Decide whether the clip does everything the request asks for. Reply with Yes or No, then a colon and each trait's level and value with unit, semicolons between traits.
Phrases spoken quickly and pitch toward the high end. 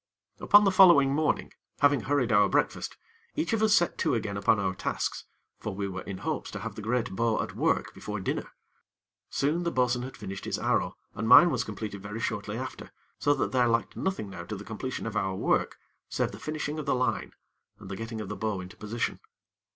No: fast, 215 wpm; low, 115 Hz